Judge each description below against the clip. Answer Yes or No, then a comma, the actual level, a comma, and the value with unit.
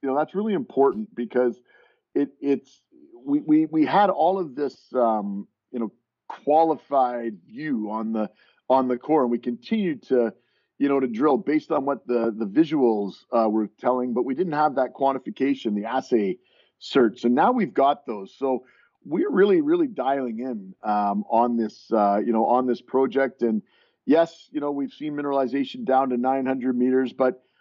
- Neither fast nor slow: Yes, average, 185 wpm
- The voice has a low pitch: Yes, low, 130 Hz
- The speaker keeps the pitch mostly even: No, average, 4.4 semitones